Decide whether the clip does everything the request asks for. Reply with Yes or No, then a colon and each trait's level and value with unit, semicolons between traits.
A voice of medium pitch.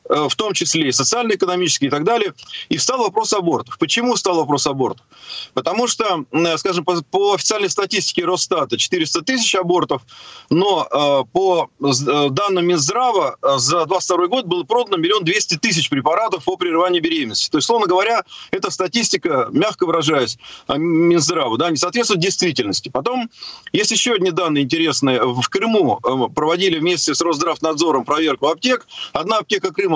Yes: medium, 180 Hz